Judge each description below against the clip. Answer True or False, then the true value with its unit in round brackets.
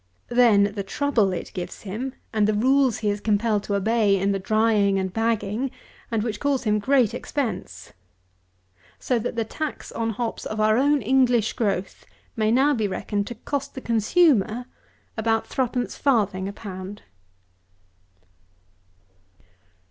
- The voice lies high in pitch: True (220 Hz)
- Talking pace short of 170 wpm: True (150 wpm)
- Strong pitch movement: False (3.4 semitones)